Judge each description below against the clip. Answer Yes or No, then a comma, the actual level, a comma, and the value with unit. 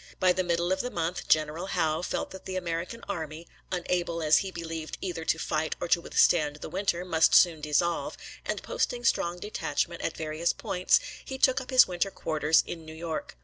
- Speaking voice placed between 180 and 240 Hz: No, medium, 170 Hz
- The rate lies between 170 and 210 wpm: Yes, average, 195 wpm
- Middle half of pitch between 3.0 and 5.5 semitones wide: No, narrow, 2.5 semitones